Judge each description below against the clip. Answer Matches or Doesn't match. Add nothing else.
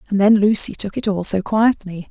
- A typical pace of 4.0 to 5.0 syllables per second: Doesn't match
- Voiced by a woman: Matches